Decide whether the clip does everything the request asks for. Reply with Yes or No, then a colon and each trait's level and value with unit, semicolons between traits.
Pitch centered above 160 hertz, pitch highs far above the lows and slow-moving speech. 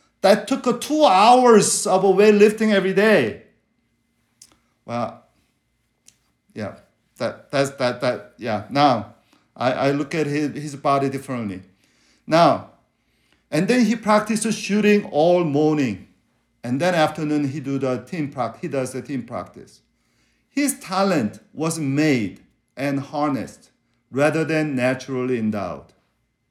No: medium, 150 Hz; wide, 7.3 semitones; slow, 125 wpm